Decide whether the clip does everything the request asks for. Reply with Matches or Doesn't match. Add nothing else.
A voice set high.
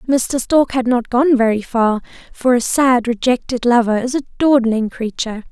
Matches